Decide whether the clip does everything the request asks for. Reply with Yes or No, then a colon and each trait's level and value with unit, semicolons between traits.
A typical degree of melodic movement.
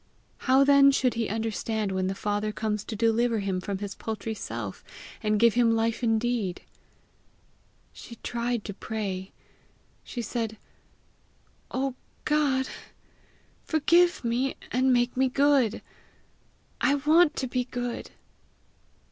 Yes: average, 3.5 semitones